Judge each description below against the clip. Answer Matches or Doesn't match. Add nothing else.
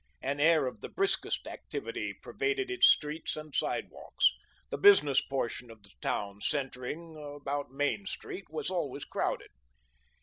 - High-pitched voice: Doesn't match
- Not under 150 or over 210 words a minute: Doesn't match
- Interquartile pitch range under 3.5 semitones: Doesn't match